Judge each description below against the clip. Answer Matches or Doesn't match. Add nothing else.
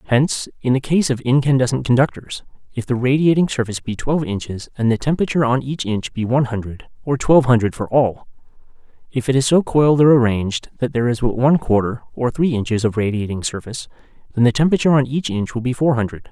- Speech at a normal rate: Doesn't match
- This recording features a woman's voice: Doesn't match